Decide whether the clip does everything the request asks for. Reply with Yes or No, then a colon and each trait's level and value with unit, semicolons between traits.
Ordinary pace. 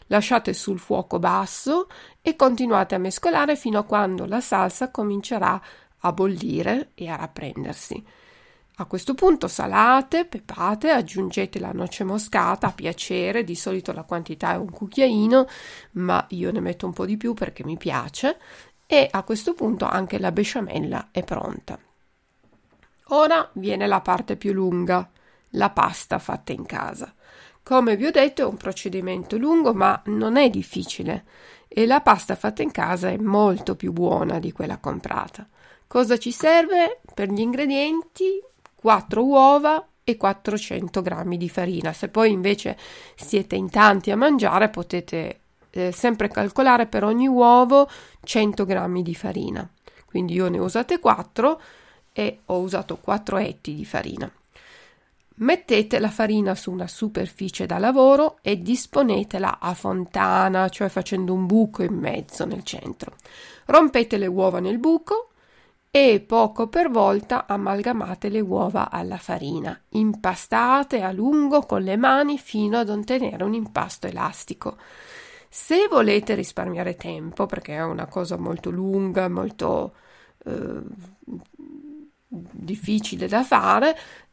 Yes: average, 140 wpm